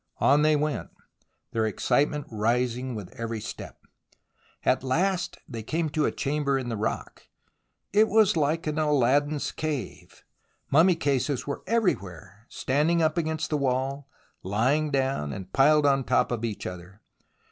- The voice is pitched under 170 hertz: Yes, medium, 140 Hz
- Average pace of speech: Yes, average, 145 wpm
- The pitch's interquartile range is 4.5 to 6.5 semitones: Yes, average, 4.8 semitones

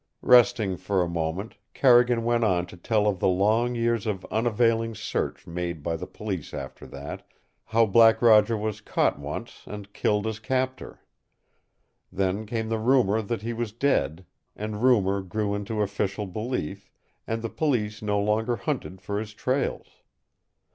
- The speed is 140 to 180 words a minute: Yes, average, 160 wpm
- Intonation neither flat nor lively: Yes, average, 3.1 semitones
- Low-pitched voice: Yes, low, 110 Hz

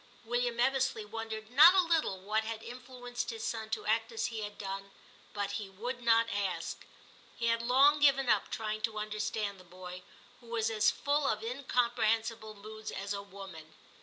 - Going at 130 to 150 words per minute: No, average, 180 wpm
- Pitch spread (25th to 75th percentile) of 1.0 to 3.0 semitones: Yes, average, 2.7 semitones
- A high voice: Yes, high, 225 Hz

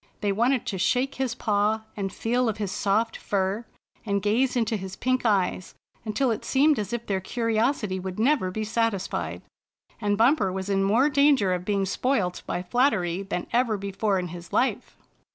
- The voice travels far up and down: No, average, 4.0 semitones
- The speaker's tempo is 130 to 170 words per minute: No, average, 180 wpm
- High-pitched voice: Yes, high, 210 Hz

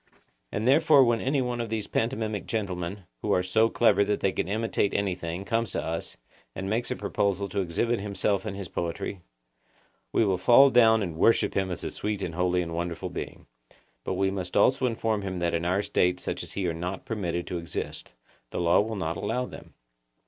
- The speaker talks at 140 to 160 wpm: No, fast, 205 wpm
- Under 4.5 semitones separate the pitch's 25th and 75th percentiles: Yes, average, 3.9 semitones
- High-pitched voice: No, low, 100 Hz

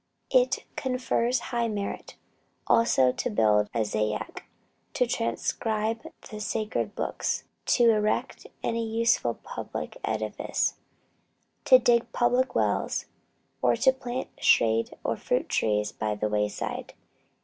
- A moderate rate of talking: No, slow, 115 wpm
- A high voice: Yes, high, 225 Hz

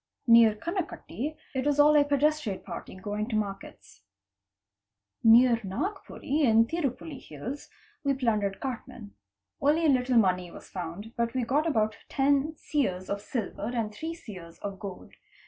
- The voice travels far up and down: Yes, wide, 5.8 semitones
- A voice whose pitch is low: No, high, 235 Hz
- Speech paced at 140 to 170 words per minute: Yes, average, 145 wpm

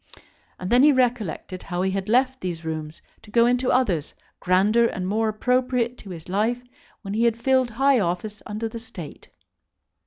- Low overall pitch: No, high, 220 Hz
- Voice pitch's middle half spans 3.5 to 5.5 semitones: Yes, average, 5.0 semitones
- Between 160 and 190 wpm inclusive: Yes, average, 180 wpm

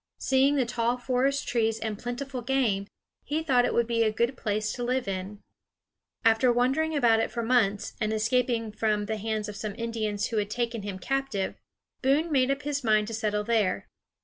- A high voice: Yes, high, 230 Hz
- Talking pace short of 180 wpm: No, average, 195 wpm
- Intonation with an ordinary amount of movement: Yes, average, 3.2 semitones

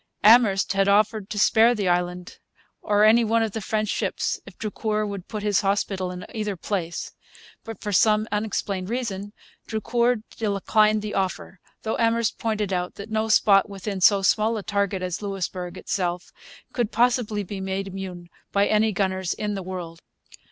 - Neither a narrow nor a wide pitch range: No, narrow, 2.2 semitones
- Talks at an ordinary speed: Yes, average, 170 wpm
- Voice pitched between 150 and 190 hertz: No, high, 205 Hz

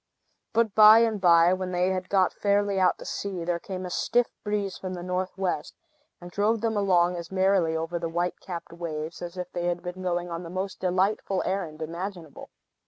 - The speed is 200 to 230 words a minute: Yes, fast, 205 wpm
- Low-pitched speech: No, medium, 185 Hz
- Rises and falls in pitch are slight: Yes, narrow, 2.2 semitones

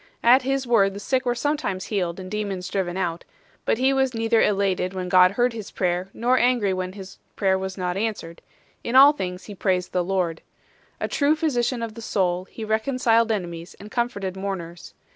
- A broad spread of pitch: No, average, 4.5 semitones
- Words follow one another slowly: No, average, 195 wpm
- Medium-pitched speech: No, high, 200 Hz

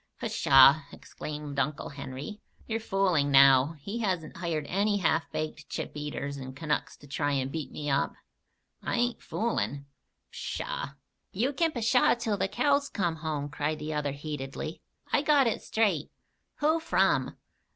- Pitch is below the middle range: No, medium, 155 Hz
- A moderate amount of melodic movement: No, wide, 7.0 semitones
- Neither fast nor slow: Yes, average, 150 wpm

